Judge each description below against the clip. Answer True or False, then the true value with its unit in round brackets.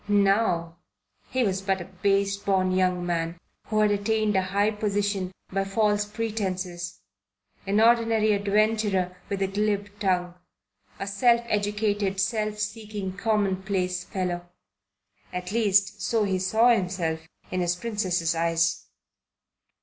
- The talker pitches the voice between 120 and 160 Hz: False (200 Hz)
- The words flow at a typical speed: False (125 wpm)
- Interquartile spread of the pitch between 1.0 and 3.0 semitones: True (2.4 semitones)